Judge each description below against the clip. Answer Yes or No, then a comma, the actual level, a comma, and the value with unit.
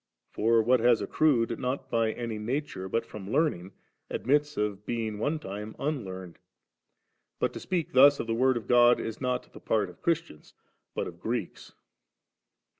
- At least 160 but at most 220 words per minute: Yes, average, 165 wpm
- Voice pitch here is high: No, low, 115 Hz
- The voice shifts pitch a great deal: No, average, 4.2 semitones